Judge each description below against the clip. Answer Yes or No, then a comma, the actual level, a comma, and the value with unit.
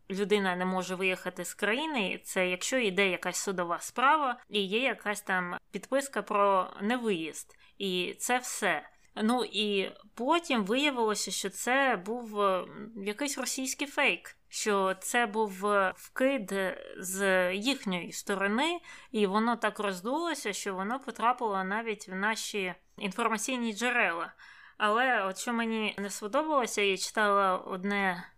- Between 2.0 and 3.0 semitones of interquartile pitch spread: No, average, 3.9 semitones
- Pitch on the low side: No, high, 210 Hz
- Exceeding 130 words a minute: No, average, 125 wpm